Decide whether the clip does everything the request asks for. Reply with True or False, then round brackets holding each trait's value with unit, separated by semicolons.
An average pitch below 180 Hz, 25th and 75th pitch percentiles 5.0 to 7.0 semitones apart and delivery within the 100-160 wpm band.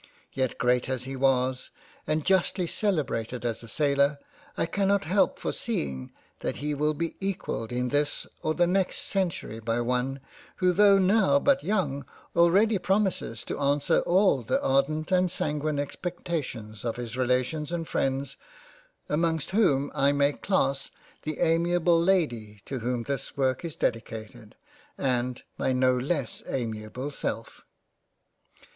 True (140 Hz; 5.5 semitones; 140 wpm)